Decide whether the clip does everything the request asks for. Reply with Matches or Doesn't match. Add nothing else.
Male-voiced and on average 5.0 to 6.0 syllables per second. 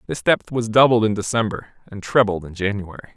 Matches